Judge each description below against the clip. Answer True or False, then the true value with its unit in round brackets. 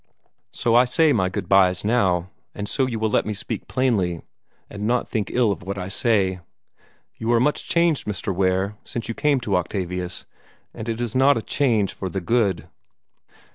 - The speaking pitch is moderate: False (105 Hz)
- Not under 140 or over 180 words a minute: False (190 wpm)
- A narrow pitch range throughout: False (4.3 semitones)